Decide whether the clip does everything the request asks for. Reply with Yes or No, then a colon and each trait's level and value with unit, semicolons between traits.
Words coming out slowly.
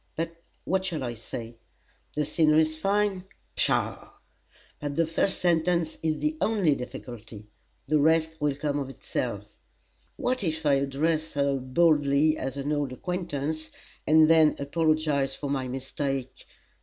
No: average, 145 wpm